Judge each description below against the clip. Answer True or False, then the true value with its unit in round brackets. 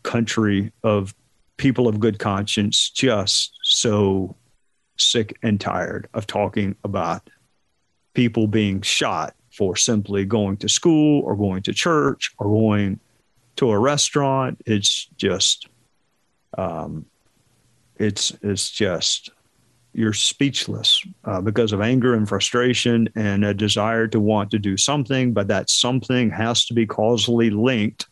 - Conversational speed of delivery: False (130 wpm)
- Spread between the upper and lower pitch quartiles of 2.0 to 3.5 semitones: True (2.6 semitones)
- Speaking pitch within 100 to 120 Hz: True (110 Hz)